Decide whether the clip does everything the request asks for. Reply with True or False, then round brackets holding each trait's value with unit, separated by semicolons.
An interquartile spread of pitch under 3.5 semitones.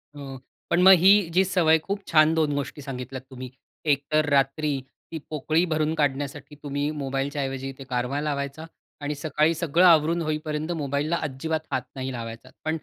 True (2.6 semitones)